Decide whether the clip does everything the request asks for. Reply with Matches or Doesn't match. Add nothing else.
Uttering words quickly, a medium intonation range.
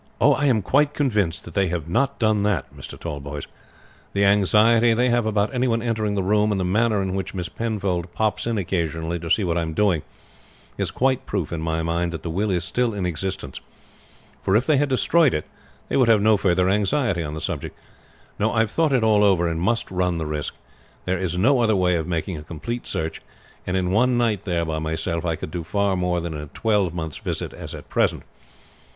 Matches